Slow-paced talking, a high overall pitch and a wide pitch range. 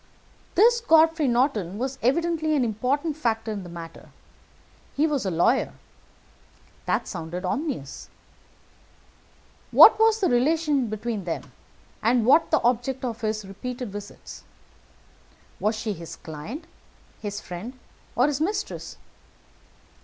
Yes: slow, 125 wpm; high, 245 Hz; wide, 6.5 semitones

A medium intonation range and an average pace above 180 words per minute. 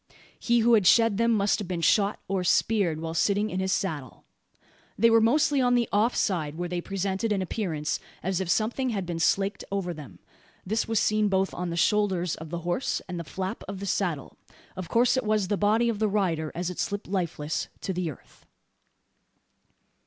Yes: average, 3.7 semitones; fast, 205 wpm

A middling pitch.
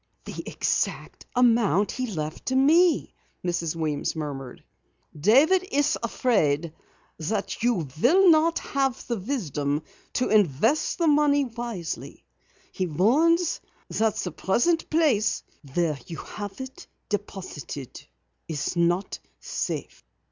No: high, 215 Hz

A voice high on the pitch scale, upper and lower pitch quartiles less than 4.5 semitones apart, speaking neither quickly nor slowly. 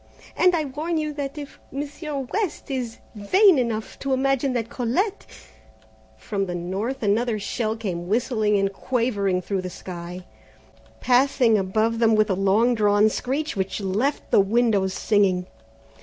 No: high, 225 Hz; average, 5.3 semitones; average, 150 wpm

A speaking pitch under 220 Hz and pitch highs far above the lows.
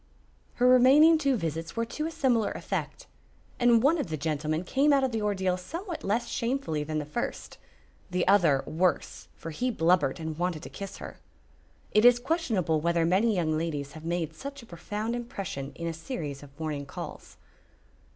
Yes: medium, 185 Hz; wide, 7.4 semitones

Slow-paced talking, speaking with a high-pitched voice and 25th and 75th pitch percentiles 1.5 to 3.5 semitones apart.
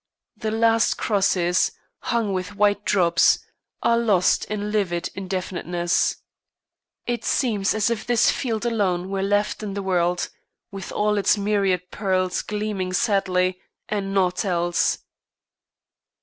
Yes: slow, 125 wpm; high, 195 Hz; narrow, 2.6 semitones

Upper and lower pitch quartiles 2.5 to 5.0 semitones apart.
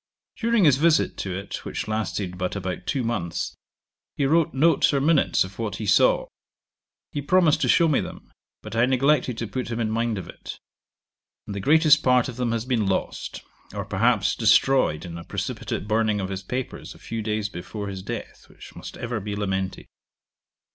No: wide, 5.4 semitones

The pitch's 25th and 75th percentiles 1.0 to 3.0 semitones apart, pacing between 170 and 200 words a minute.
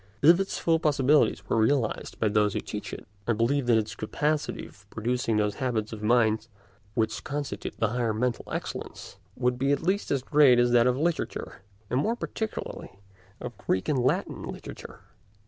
No: average, 4.6 semitones; average, 180 wpm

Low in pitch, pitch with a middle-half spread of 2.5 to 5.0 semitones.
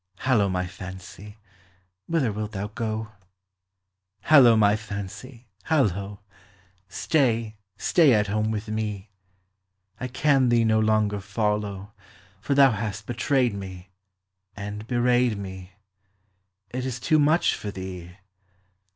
Yes: low, 110 Hz; average, 3.3 semitones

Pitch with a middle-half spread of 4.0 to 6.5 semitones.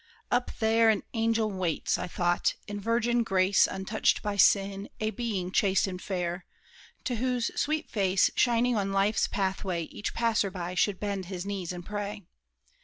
No: average, 3.1 semitones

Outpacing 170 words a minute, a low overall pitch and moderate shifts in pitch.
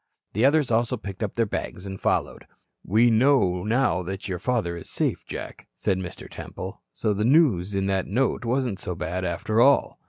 Yes: average, 190 wpm; low, 105 Hz; average, 4.6 semitones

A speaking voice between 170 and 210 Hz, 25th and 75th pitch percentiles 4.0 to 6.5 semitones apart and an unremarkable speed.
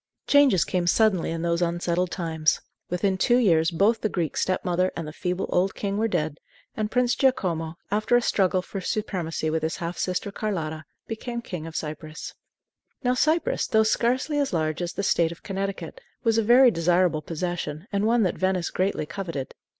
Yes: medium, 185 Hz; average, 4.6 semitones; average, 185 wpm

